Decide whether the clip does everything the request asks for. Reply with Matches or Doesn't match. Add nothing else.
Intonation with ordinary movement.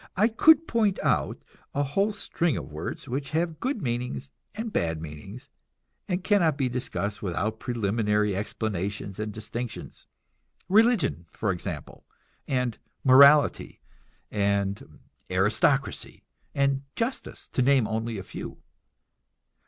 Doesn't match